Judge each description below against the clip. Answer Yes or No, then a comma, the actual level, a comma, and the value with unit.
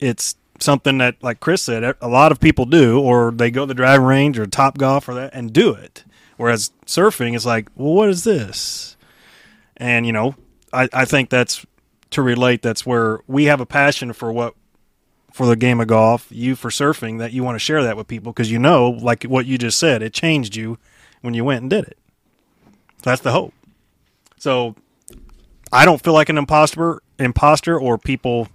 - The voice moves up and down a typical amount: Yes, average, 3.1 semitones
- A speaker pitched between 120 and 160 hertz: Yes, low, 125 Hz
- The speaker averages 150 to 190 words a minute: No, fast, 205 wpm